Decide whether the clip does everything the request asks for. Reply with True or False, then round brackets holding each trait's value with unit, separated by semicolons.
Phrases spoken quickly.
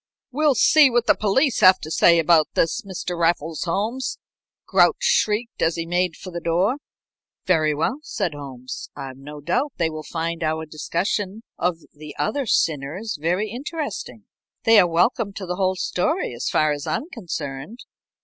False (170 wpm)